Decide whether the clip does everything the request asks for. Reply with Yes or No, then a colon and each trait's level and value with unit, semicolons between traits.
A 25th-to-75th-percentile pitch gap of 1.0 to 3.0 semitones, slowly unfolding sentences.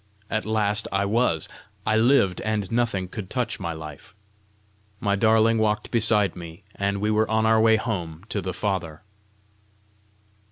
No: average, 2.7 semitones; average, 155 wpm